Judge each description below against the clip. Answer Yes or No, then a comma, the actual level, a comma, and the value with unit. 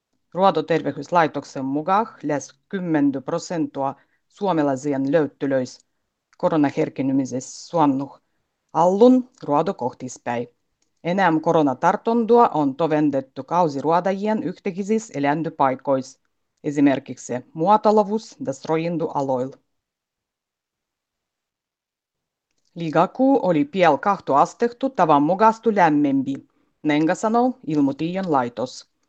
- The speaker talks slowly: Yes, slow, 75 wpm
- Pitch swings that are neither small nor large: No, wide, 6.1 semitones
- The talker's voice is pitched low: No, medium, 160 Hz